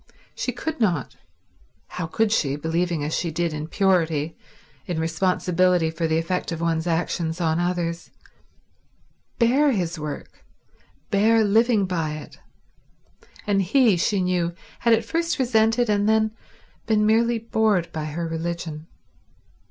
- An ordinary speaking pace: No, slow, 130 wpm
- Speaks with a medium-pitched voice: Yes, medium, 180 Hz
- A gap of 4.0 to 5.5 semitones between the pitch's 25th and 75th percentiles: Yes, average, 5.1 semitones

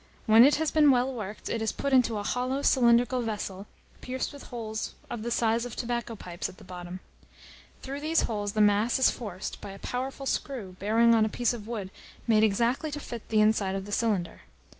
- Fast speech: Yes, fast, 210 wpm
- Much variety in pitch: No, average, 3.4 semitones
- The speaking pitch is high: Yes, high, 230 Hz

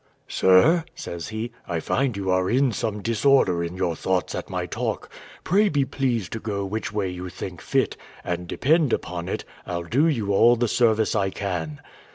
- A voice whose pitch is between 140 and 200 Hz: No, low, 105 Hz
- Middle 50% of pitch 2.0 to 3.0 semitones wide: No, average, 5.0 semitones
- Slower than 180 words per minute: No, average, 190 wpm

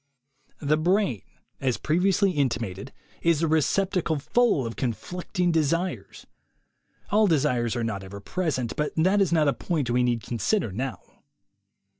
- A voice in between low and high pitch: Yes, medium, 150 Hz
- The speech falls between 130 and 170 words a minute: Yes, average, 145 wpm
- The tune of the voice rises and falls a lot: Yes, wide, 6.7 semitones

